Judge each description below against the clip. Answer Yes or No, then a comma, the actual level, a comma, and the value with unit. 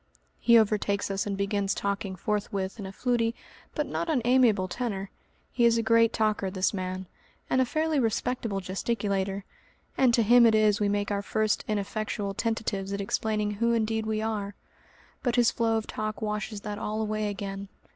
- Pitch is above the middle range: Yes, high, 215 Hz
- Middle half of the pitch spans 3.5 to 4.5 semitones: No, narrow, 2.4 semitones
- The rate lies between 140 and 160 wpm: No, average, 175 wpm